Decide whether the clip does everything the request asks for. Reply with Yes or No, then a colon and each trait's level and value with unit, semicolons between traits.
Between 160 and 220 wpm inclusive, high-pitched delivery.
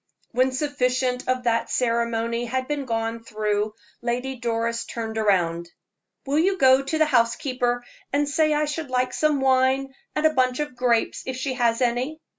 Yes: average, 170 wpm; very high, 255 Hz